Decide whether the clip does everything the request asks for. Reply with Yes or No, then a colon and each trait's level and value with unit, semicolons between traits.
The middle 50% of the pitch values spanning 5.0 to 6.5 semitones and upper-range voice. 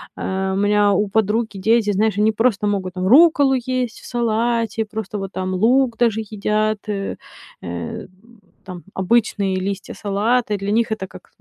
No: average, 2.9 semitones; high, 210 Hz